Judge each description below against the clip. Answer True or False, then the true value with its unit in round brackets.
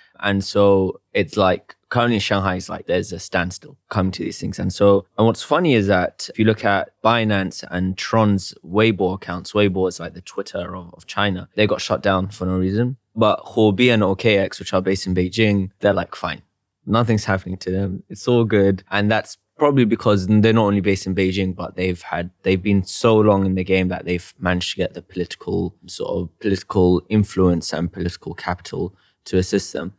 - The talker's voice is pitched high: False (95 Hz)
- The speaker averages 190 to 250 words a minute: True (205 wpm)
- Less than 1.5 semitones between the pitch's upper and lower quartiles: False (2.5 semitones)